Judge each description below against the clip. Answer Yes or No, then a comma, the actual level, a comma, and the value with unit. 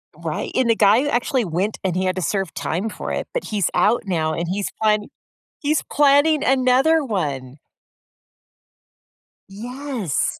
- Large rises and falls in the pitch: Yes, wide, 6.4 semitones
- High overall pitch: Yes, high, 215 Hz